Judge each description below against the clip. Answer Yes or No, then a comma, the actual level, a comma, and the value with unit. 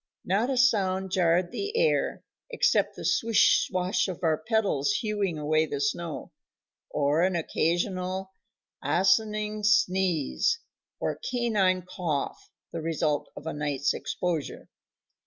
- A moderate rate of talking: No, slow, 120 wpm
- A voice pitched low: No, medium, 185 Hz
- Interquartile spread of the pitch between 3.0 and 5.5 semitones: Yes, average, 4.8 semitones